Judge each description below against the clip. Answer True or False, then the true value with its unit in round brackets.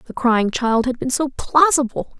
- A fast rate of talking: False (190 wpm)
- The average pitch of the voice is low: False (260 Hz)